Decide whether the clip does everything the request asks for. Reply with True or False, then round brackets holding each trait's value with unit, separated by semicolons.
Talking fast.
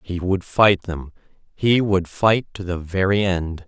False (165 wpm)